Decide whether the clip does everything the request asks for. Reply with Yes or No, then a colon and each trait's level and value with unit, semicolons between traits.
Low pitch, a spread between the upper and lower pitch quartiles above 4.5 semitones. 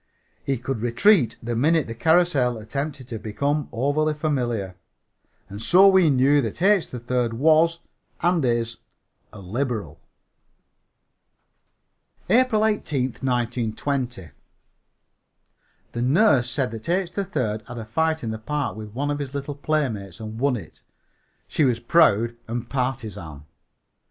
Yes: low, 130 Hz; average, 5.1 semitones